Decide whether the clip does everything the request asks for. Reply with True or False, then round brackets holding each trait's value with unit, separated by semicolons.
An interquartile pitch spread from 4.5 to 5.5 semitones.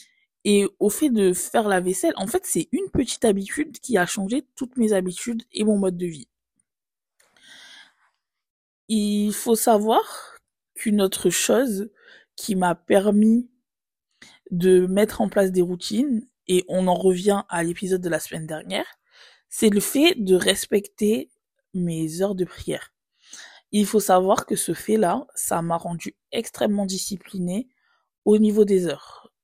False (3.8 semitones)